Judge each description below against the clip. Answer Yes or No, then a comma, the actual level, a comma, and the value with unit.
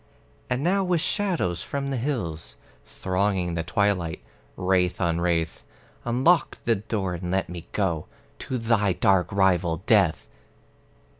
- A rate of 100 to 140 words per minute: Yes, slow, 135 wpm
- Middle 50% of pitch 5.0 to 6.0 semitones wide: Yes, average, 5.3 semitones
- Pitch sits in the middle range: No, very low, 95 Hz